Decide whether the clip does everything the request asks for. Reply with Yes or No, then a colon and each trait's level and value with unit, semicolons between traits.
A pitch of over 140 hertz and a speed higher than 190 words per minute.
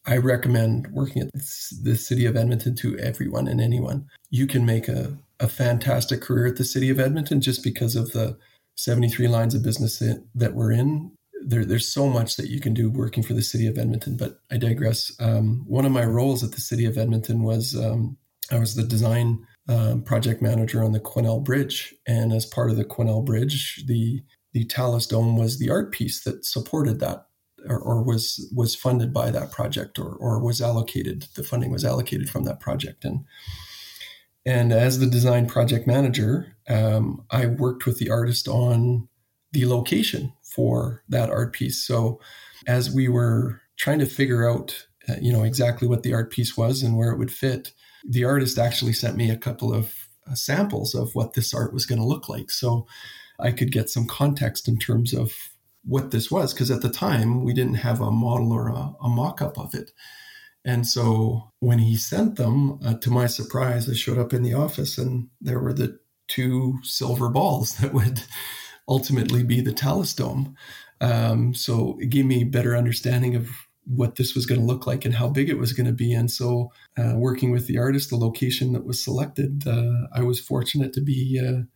No: low, 120 Hz; average, 200 wpm